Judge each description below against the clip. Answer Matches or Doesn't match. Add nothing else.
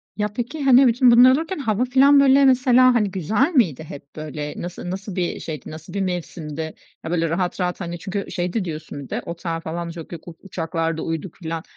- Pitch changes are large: Matches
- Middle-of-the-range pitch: Matches